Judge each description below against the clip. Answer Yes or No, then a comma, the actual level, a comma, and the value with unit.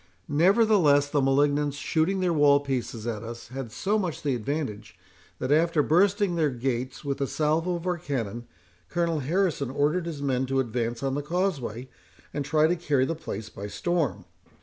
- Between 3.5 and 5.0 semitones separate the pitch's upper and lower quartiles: Yes, average, 4.6 semitones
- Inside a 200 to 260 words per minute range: No, average, 175 wpm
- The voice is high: No, medium, 145 Hz